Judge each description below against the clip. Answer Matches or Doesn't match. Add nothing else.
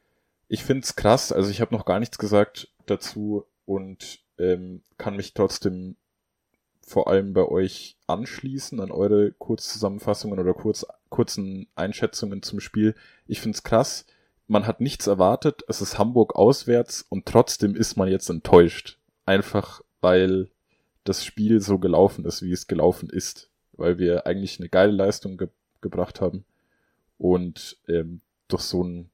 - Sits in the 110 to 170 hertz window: Doesn't match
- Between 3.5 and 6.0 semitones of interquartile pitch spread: Doesn't match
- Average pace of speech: Matches